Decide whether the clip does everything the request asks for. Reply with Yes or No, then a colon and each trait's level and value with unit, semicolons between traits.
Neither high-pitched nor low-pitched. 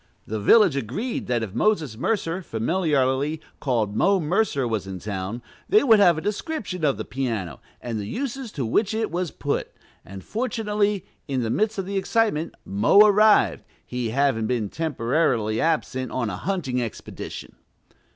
Yes: medium, 145 Hz